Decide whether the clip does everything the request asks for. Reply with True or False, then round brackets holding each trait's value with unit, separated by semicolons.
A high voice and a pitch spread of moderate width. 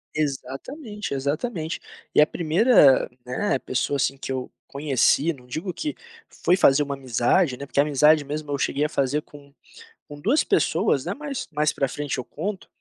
False (145 Hz; 3.8 semitones)